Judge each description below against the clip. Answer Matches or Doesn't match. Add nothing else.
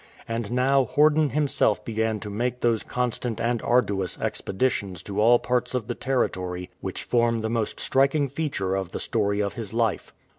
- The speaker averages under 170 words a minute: Doesn't match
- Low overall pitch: Matches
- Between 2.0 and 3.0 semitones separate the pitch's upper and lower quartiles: Doesn't match